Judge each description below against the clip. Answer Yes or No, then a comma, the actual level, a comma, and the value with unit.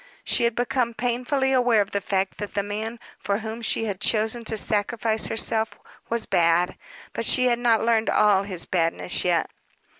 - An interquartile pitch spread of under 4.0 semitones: Yes, average, 2.8 semitones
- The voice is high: Yes, high, 220 Hz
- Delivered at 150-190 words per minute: Yes, average, 180 wpm